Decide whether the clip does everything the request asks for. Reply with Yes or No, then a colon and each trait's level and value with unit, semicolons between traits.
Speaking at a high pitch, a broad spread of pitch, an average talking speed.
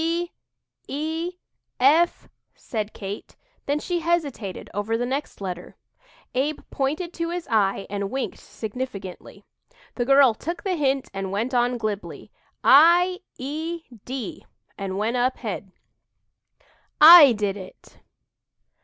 No: very high, 260 Hz; wide, 7.5 semitones; slow, 125 wpm